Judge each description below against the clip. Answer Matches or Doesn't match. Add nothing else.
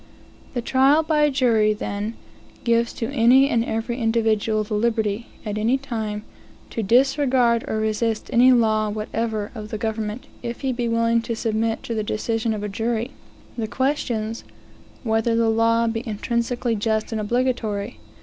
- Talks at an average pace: Matches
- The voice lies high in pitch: Matches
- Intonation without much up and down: Matches